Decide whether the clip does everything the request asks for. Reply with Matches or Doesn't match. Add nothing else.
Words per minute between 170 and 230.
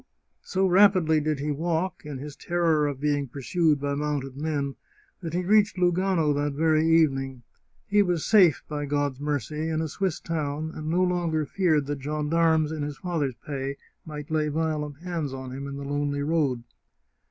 Matches